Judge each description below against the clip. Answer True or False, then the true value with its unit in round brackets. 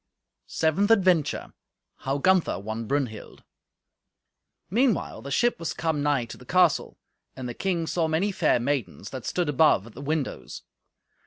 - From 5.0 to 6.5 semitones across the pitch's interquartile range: True (5.3 semitones)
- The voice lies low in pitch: False (150 Hz)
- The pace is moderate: True (150 wpm)